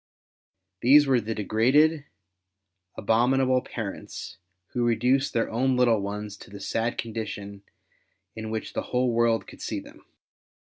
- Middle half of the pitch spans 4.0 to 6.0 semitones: No, average, 2.7 semitones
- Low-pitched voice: Yes, low, 115 Hz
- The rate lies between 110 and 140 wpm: Yes, slow, 135 wpm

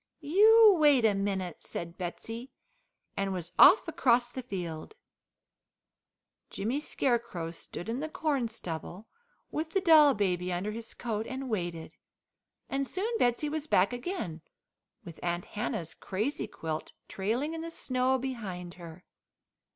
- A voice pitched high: Yes, high, 230 Hz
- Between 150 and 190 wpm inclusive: No, slow, 135 wpm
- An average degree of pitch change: No, wide, 7.4 semitones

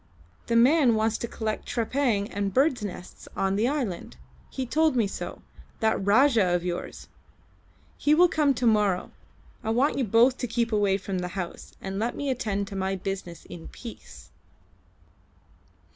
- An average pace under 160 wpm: No, average, 165 wpm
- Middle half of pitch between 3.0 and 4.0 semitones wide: No, average, 4.5 semitones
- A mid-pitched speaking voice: No, high, 220 Hz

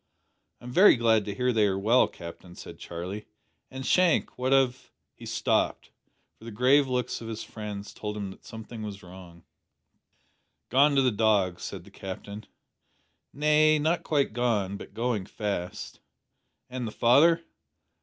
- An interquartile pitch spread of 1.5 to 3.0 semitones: No, average, 4.3 semitones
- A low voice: Yes, low, 115 Hz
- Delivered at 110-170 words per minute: Yes, average, 160 wpm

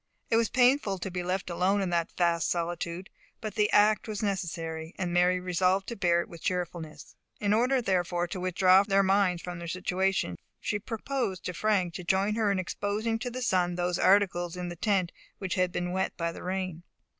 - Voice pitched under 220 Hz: Yes, medium, 185 Hz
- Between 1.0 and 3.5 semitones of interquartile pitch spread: Yes, narrow, 2.5 semitones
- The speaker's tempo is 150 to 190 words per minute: No, average, 200 wpm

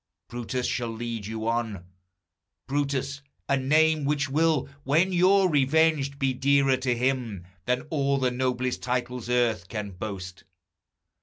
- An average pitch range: Yes, average, 3.1 semitones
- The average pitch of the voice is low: Yes, low, 130 Hz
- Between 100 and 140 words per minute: Yes, slow, 135 wpm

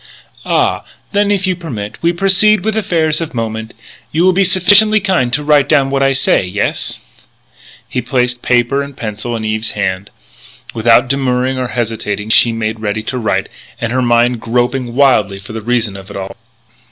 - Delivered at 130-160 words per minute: No, average, 175 wpm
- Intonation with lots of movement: Yes, wide, 5.7 semitones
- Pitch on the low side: Yes, low, 125 Hz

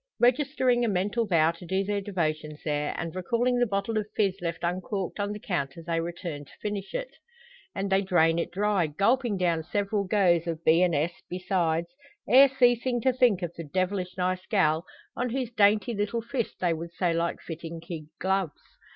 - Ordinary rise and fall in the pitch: Yes, average, 4.0 semitones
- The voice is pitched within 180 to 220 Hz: Yes, medium, 185 Hz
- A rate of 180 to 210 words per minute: Yes, average, 190 wpm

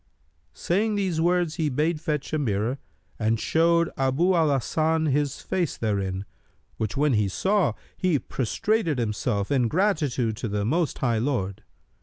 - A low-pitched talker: No, medium, 145 Hz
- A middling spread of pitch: No, wide, 6.8 semitones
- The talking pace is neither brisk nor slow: Yes, average, 150 wpm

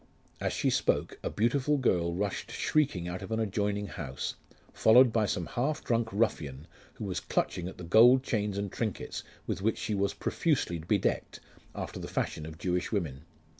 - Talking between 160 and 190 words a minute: Yes, average, 175 wpm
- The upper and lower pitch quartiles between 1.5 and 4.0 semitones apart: No, average, 4.7 semitones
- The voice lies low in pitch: Yes, low, 100 Hz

